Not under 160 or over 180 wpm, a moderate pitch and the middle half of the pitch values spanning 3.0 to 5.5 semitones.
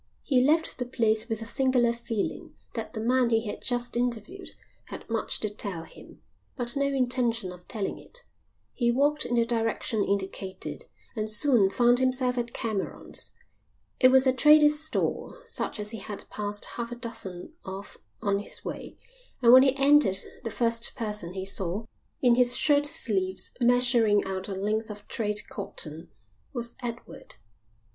No: average, 165 wpm; high, 235 Hz; average, 3.6 semitones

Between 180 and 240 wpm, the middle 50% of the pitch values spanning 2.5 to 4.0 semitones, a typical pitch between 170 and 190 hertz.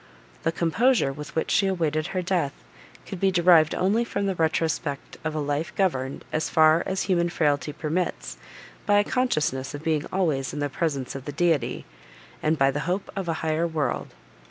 No: average, 185 wpm; average, 3.7 semitones; medium, 160 Hz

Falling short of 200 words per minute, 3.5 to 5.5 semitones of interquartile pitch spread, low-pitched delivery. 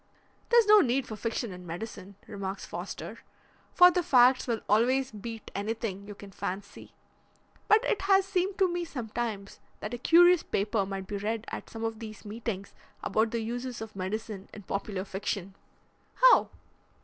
No: average, 165 wpm; average, 4.4 semitones; high, 225 Hz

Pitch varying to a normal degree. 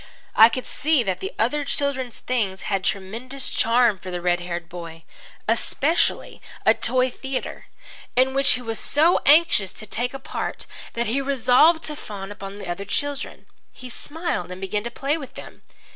No: wide, 6.0 semitones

